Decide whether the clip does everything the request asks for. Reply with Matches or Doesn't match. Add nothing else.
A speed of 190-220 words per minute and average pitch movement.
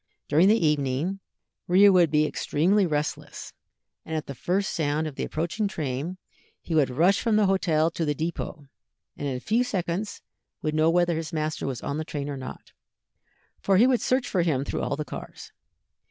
Matches